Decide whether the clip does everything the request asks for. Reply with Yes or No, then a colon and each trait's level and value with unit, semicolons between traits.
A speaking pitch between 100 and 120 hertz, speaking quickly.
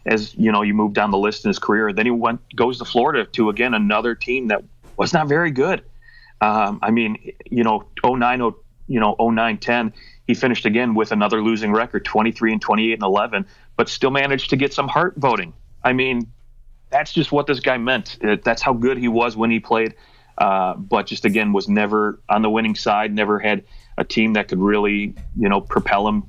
Yes: low, 115 Hz; fast, 220 wpm